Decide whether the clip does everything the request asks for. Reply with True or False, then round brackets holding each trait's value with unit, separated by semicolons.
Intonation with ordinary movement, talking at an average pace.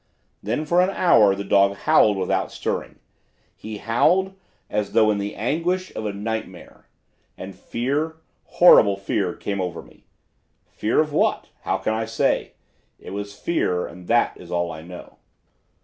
False (5.9 semitones; 160 wpm)